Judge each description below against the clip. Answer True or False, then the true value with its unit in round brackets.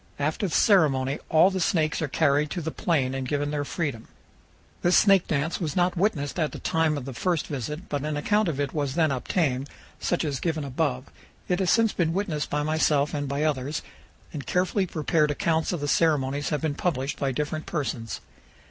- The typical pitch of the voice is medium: True (150 Hz)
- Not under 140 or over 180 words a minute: False (205 wpm)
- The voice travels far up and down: False (3.0 semitones)